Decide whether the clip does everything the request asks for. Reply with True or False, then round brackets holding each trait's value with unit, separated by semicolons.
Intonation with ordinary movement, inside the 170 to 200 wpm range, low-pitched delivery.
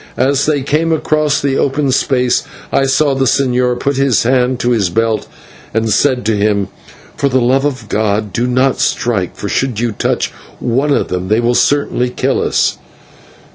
True (3.5 semitones; 180 wpm; 125 Hz)